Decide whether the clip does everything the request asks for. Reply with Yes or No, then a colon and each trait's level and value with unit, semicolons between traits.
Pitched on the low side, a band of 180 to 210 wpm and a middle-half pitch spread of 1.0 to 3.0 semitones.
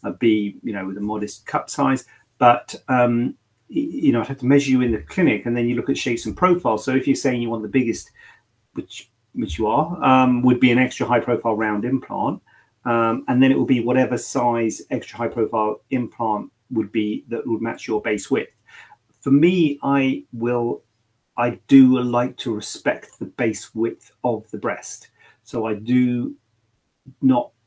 Yes: low, 120 Hz; average, 190 wpm; average, 2.7 semitones